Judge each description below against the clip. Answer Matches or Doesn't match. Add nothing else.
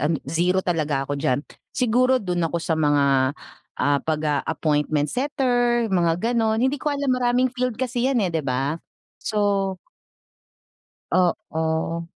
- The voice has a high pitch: Doesn't match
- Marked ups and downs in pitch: Matches